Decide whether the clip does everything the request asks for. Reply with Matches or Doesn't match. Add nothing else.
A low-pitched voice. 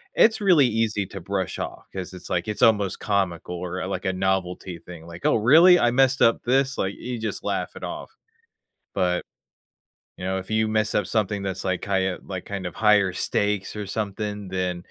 Matches